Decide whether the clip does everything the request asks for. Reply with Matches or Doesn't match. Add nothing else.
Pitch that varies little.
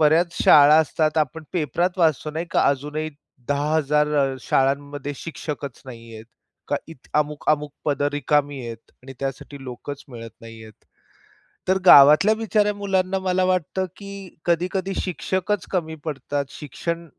Doesn't match